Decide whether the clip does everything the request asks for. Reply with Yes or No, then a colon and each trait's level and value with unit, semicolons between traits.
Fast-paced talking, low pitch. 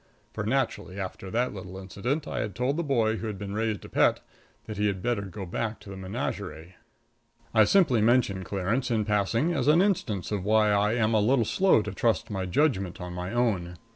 Yes: fast, 210 wpm; low, 105 Hz